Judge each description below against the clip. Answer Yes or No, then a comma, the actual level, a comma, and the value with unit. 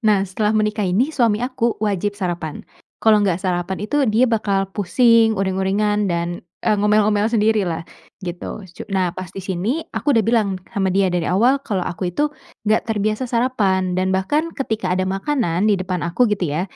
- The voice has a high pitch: Yes, high, 205 Hz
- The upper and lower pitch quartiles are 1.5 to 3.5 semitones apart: Yes, average, 3.1 semitones